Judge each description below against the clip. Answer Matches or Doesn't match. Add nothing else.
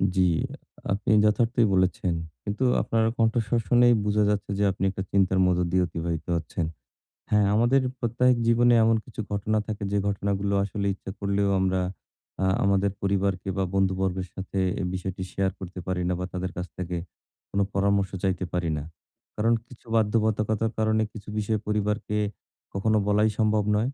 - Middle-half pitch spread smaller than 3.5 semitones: Matches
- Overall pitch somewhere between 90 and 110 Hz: Matches